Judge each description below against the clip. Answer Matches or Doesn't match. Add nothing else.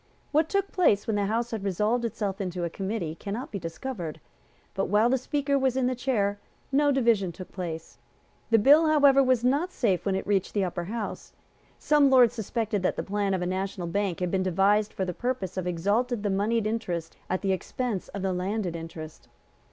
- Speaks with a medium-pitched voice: Doesn't match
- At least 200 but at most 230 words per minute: Matches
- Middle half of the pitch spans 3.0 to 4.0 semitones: Doesn't match